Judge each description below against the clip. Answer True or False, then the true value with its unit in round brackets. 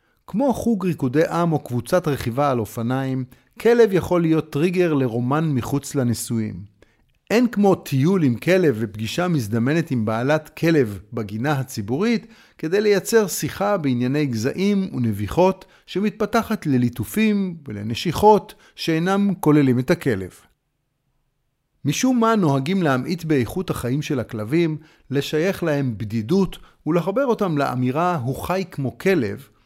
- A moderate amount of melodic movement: False (6.5 semitones)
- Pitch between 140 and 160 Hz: True (150 Hz)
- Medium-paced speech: True (120 wpm)